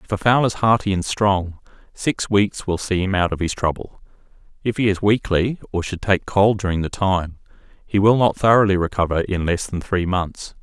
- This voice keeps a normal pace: No, fast, 210 wpm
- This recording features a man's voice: Yes, male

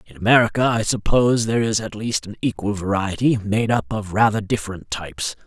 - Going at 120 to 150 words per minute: No, average, 185 wpm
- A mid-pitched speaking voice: No, low, 105 Hz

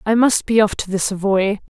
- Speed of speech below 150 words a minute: No, fast, 235 wpm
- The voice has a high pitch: Yes, high, 205 Hz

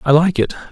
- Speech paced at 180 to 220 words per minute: No, fast, 250 wpm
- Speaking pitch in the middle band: Yes, medium, 155 Hz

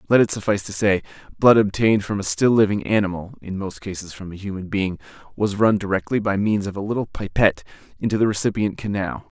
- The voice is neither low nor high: No, low, 100 Hz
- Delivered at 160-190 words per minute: No, fast, 205 wpm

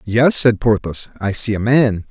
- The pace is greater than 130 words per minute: Yes, average, 200 wpm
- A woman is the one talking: No, male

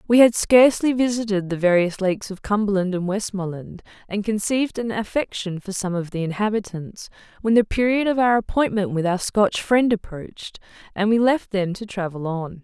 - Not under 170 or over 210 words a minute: Yes, average, 180 wpm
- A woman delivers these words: Yes, female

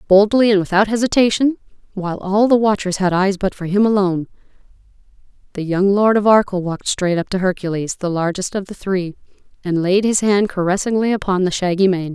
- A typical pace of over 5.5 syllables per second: Yes, 5.9 syllables/s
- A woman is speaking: Yes, female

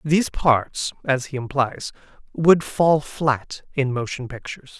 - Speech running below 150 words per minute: Yes, average, 140 wpm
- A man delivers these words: Yes, male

